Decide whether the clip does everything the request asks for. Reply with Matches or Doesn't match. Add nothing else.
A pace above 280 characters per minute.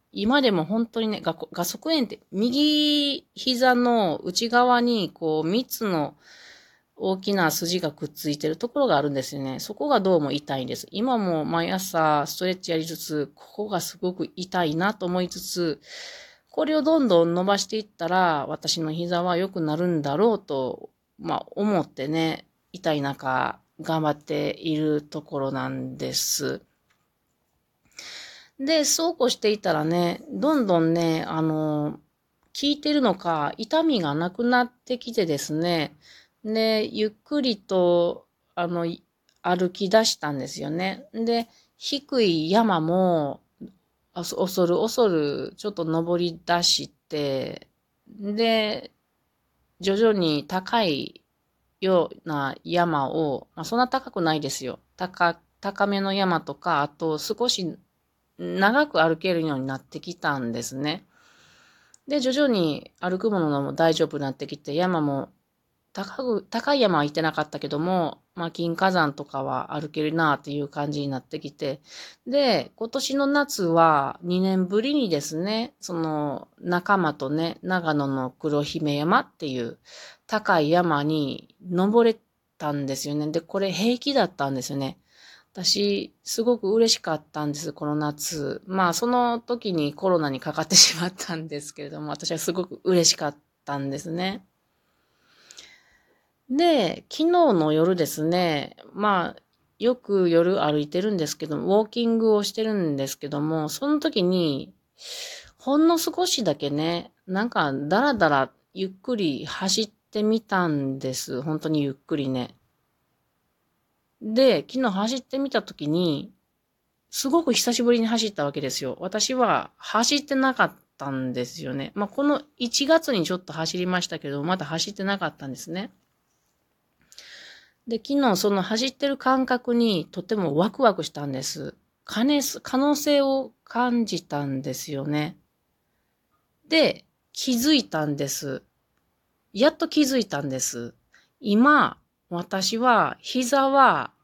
Doesn't match